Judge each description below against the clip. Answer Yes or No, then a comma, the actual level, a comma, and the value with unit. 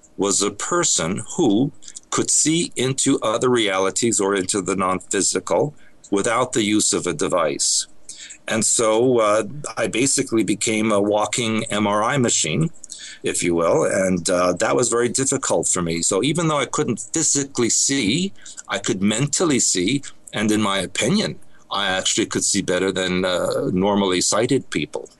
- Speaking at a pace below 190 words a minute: Yes, average, 155 wpm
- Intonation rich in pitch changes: No, average, 4.5 semitones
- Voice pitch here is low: Yes, low, 105 Hz